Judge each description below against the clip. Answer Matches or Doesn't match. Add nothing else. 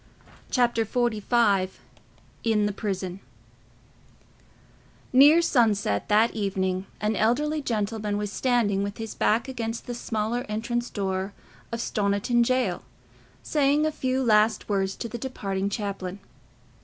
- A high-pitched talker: Matches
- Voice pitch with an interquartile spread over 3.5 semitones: Doesn't match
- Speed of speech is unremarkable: Doesn't match